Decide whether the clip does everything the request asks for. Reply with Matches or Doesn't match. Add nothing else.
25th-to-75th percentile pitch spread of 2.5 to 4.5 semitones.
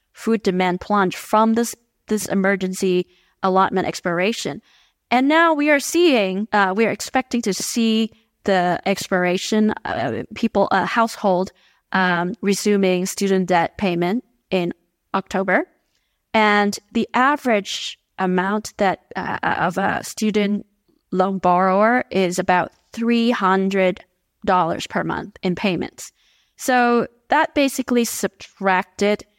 Matches